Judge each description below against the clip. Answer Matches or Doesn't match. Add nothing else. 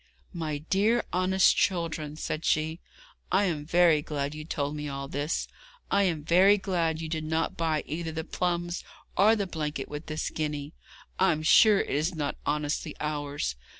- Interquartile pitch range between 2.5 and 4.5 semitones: Matches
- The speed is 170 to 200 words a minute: Matches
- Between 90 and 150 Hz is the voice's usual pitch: Doesn't match